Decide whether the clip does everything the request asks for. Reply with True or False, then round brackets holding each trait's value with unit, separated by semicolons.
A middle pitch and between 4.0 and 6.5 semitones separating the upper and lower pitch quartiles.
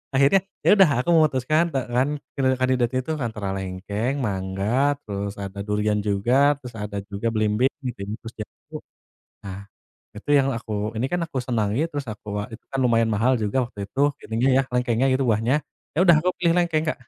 False (120 Hz; 4.4 semitones)